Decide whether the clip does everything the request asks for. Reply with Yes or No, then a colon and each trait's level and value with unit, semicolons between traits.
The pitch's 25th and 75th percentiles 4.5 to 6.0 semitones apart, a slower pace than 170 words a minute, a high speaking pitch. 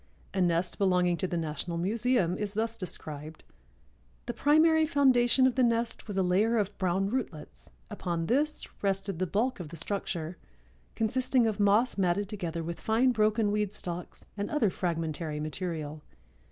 Yes: average, 5.1 semitones; average, 160 wpm; high, 195 Hz